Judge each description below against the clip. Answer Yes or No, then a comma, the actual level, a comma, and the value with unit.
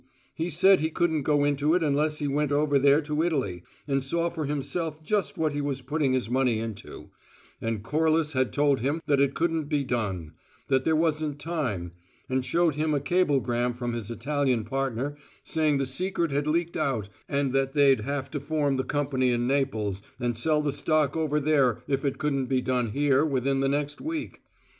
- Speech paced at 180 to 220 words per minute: Yes, average, 195 wpm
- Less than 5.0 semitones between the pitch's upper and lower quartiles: Yes, average, 2.9 semitones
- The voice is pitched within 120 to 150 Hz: Yes, medium, 140 Hz